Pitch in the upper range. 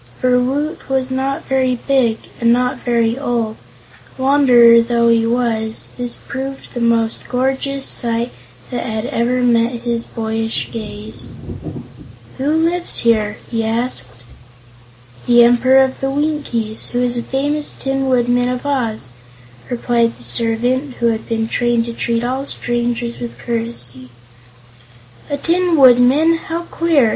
Yes: high, 245 Hz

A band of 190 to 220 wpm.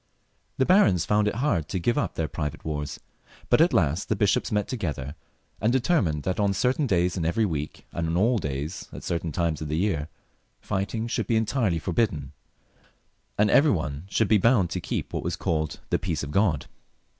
Yes: average, 200 wpm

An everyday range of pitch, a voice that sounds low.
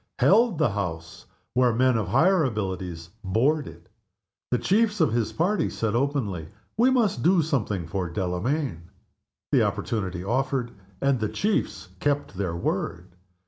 No: wide, 8.4 semitones; low, 120 Hz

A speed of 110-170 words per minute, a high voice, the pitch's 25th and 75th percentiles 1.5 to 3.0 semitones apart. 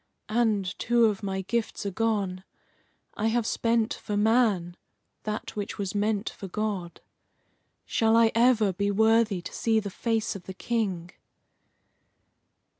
Yes: average, 140 wpm; high, 215 Hz; narrow, 2.5 semitones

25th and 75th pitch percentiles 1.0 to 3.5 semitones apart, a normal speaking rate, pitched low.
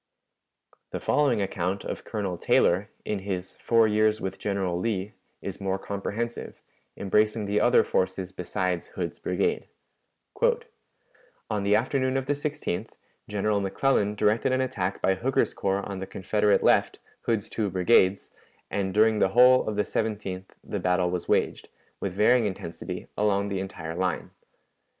Yes: average, 2.8 semitones; average, 150 wpm; low, 100 Hz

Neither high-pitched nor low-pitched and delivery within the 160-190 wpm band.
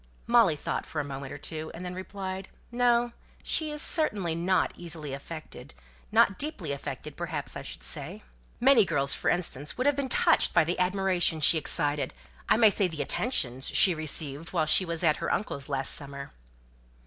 Yes: medium, 170 Hz; average, 185 wpm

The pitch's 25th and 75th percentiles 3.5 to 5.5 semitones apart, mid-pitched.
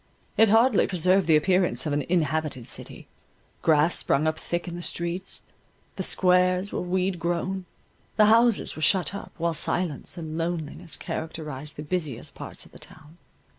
No: average, 3.0 semitones; medium, 170 Hz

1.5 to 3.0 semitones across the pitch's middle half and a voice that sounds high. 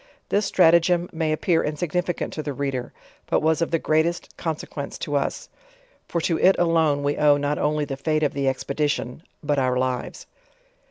No: average, 2.7 semitones; medium, 150 Hz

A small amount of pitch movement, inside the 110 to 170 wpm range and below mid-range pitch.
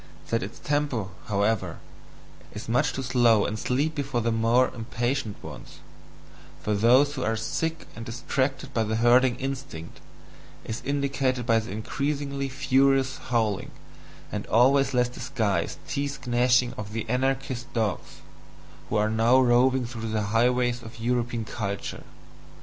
No: average, 3.0 semitones; average, 140 wpm; low, 120 Hz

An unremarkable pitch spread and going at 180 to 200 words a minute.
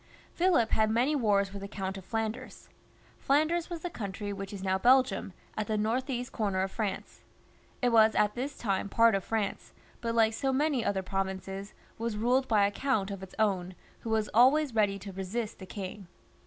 Yes: average, 3.7 semitones; average, 195 wpm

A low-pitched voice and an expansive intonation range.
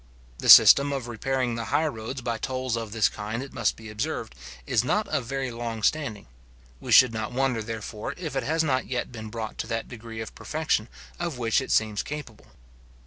No: low, 120 Hz; average, 3.4 semitones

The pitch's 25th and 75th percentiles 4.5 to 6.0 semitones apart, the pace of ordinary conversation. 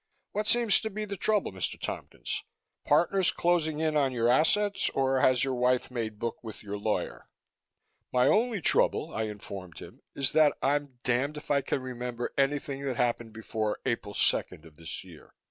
Yes: average, 5.2 semitones; average, 180 wpm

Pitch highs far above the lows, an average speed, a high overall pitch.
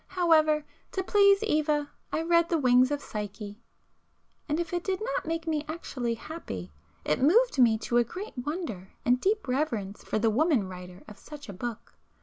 Yes: wide, 6.9 semitones; average, 175 wpm; very high, 290 Hz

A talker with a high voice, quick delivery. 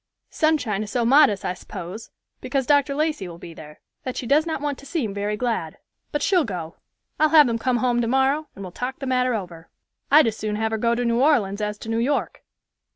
Yes: high, 240 Hz; fast, 225 wpm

